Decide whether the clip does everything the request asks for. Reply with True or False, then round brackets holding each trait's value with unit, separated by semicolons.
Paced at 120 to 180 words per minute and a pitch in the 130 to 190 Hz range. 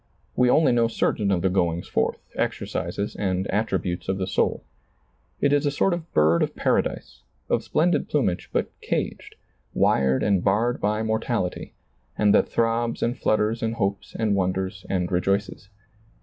False (165 wpm; 100 Hz)